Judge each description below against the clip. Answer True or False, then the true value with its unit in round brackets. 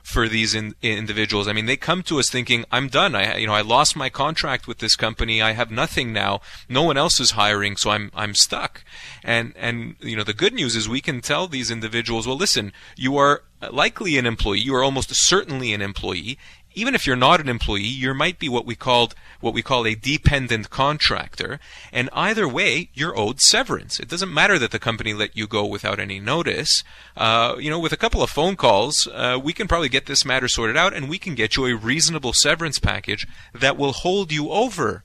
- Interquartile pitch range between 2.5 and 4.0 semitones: False (4.6 semitones)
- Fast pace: True (225 wpm)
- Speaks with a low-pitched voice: True (120 Hz)